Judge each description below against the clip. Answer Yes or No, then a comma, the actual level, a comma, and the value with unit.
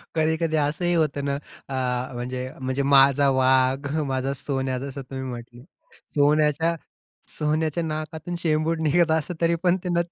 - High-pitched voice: No, medium, 145 Hz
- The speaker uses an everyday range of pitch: Yes, average, 3.3 semitones